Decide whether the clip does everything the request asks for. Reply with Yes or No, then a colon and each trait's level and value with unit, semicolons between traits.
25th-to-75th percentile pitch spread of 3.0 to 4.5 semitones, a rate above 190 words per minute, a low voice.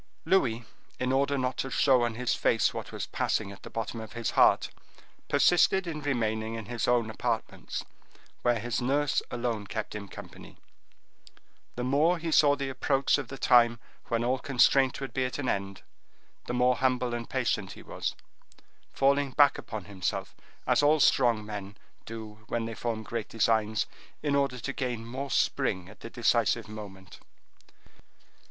No: average, 3.5 semitones; average, 170 wpm; low, 120 Hz